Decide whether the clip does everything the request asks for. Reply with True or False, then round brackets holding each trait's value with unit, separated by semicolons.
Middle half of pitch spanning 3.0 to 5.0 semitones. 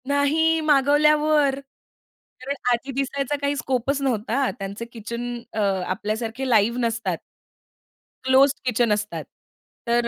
True (3.4 semitones)